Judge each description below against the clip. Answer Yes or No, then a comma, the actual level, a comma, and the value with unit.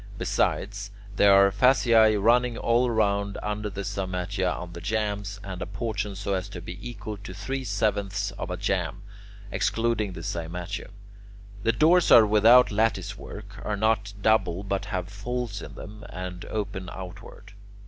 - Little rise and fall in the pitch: Yes, narrow, 2.3 semitones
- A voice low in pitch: Yes, low, 100 Hz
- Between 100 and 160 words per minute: Yes, average, 155 wpm